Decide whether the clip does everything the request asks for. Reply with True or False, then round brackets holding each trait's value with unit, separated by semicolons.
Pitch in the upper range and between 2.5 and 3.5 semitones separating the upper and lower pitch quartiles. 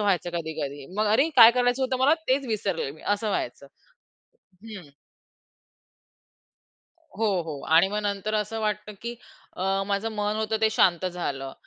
False (210 Hz; 4.2 semitones)